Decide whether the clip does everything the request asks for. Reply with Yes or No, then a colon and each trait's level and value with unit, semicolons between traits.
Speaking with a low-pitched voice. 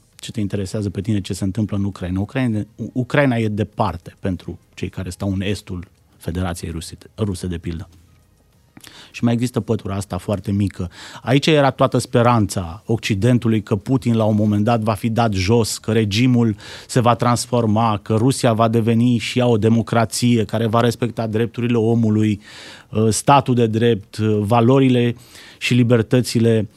Yes: low, 110 Hz